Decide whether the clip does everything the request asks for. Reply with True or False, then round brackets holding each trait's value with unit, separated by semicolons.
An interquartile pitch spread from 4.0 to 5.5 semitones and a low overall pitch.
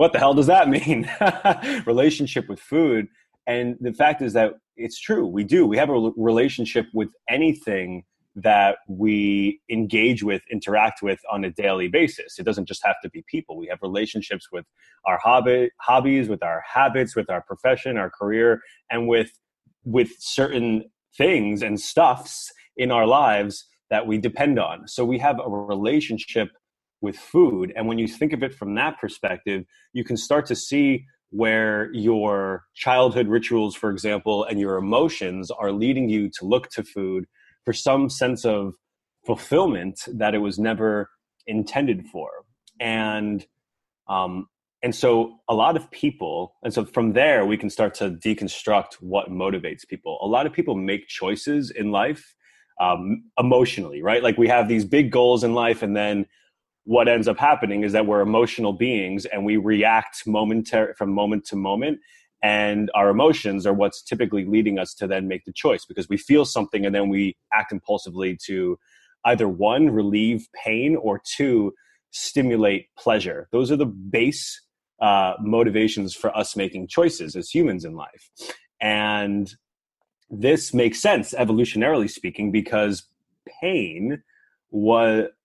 False (3.3 semitones; 110 Hz)